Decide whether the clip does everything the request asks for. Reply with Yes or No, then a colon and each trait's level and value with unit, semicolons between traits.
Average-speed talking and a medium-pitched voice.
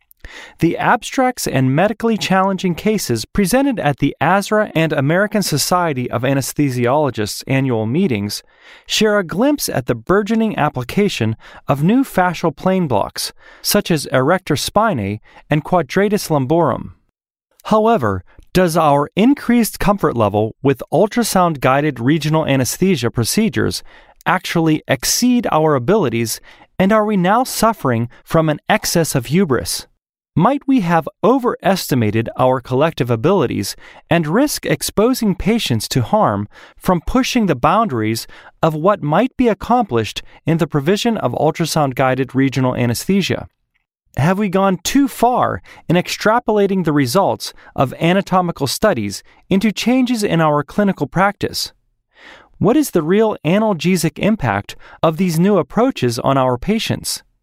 No: slow, 125 wpm; medium, 170 Hz